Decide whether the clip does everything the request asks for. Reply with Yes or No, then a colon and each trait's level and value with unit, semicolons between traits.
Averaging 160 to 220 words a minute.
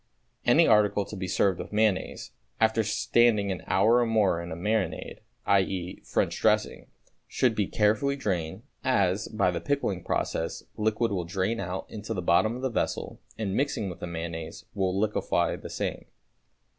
Yes: average, 170 wpm